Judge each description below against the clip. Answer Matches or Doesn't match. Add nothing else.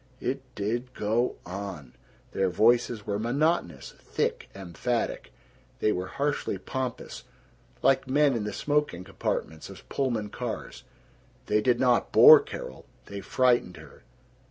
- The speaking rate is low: Matches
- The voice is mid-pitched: Doesn't match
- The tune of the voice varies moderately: Matches